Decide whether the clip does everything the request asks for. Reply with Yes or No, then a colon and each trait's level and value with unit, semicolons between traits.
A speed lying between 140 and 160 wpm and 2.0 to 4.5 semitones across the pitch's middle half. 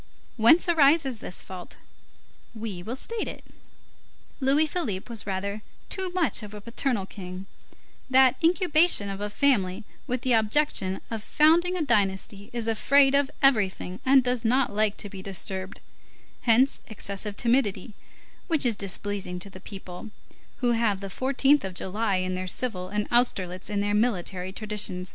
No: average, 155 wpm; wide, 5.4 semitones